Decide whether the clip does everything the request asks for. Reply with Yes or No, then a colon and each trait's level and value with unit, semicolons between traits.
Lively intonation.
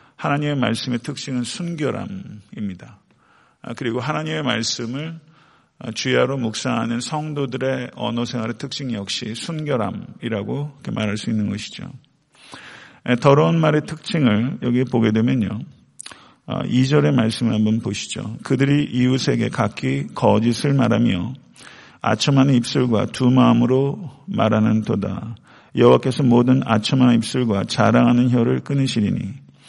No: average, 3.5 semitones